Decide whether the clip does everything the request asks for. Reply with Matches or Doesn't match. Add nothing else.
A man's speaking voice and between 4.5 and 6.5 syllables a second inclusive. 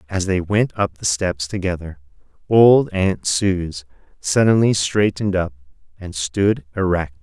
Doesn't match